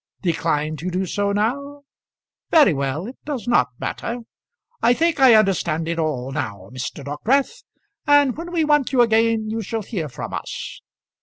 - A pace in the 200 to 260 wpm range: No, average, 165 wpm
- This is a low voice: No, high, 215 Hz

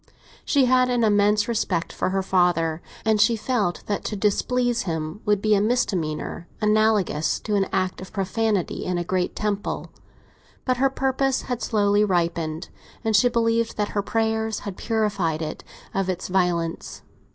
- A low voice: No, high, 205 Hz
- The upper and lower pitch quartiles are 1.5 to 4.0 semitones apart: Yes, average, 3.7 semitones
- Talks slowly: No, average, 165 wpm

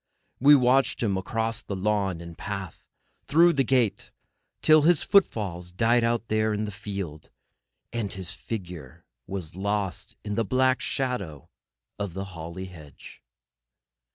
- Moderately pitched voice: No, low, 105 Hz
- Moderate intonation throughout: Yes, average, 4.4 semitones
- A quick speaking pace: No, average, 145 wpm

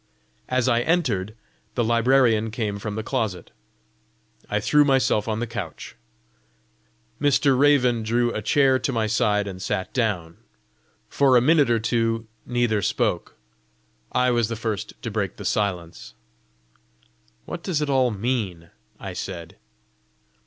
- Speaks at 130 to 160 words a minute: Yes, average, 140 wpm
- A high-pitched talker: No, low, 115 Hz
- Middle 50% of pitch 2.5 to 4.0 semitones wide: Yes, average, 3.6 semitones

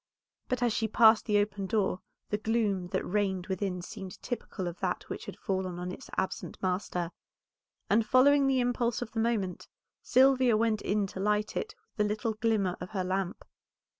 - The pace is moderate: Yes, average, 185 wpm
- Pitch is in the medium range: No, high, 210 Hz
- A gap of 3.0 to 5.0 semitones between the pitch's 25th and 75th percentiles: Yes, average, 3.5 semitones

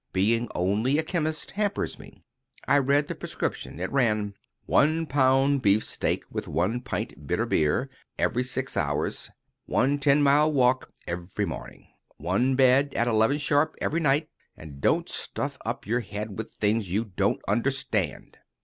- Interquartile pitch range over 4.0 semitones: Yes, wide, 5.5 semitones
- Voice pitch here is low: Yes, low, 125 Hz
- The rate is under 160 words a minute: Yes, average, 150 wpm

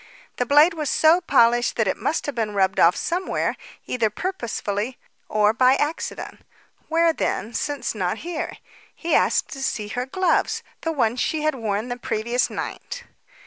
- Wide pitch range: Yes, wide, 6.3 semitones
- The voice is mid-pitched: No, very high, 250 Hz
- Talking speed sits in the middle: Yes, average, 165 wpm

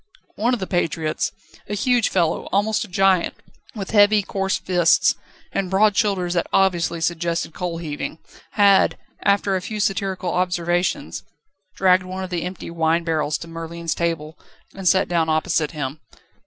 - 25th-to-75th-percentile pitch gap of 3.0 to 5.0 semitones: No, narrow, 2.6 semitones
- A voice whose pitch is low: No, medium, 180 Hz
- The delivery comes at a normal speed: Yes, average, 155 wpm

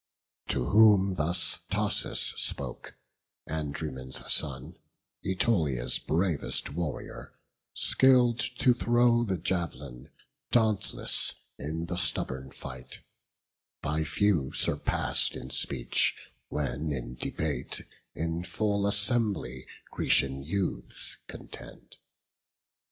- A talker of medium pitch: No, very low, 80 Hz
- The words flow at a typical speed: No, slow, 90 wpm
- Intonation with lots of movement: Yes, wide, 6.8 semitones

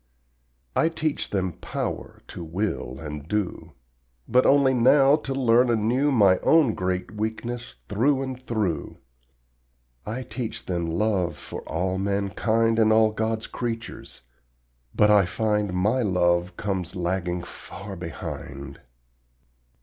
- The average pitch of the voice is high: No, low, 105 Hz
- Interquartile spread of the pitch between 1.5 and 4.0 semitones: No, average, 4.7 semitones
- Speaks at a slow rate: Yes, slow, 125 wpm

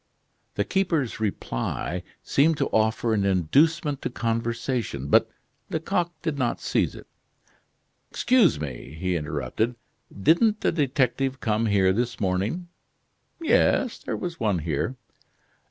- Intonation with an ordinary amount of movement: No, wide, 8.8 semitones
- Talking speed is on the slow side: Yes, slow, 120 wpm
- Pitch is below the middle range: Yes, low, 120 Hz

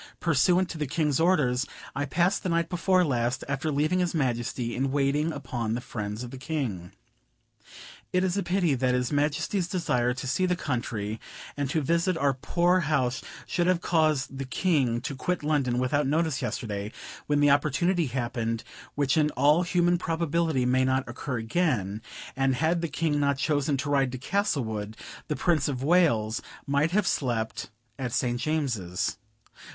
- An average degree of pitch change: Yes, average, 4.9 semitones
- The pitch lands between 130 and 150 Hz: Yes, medium, 140 Hz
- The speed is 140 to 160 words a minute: No, average, 170 wpm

